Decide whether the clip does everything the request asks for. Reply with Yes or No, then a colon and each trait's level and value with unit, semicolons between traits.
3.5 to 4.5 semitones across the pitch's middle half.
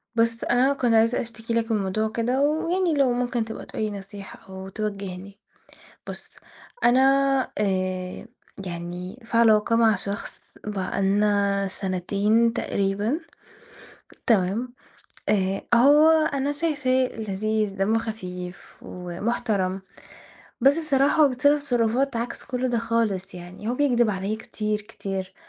Yes: average, 3.9 semitones